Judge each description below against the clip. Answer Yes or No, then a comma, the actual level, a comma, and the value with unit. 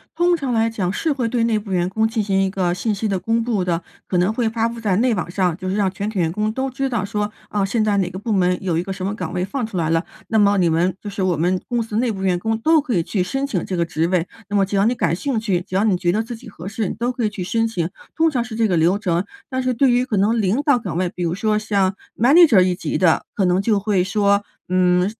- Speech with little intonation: No, average, 3.8 semitones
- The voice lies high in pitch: Yes, high, 205 Hz